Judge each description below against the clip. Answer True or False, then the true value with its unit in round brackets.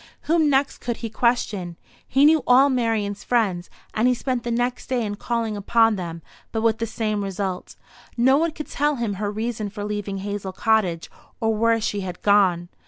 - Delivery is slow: False (190 wpm)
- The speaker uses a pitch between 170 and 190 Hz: False (220 Hz)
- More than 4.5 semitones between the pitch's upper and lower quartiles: False (3.2 semitones)